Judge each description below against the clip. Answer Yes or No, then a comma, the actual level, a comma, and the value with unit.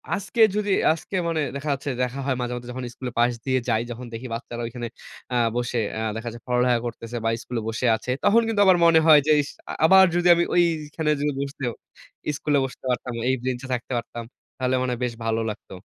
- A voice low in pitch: Yes, low, 125 Hz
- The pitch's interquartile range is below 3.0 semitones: No, average, 4.2 semitones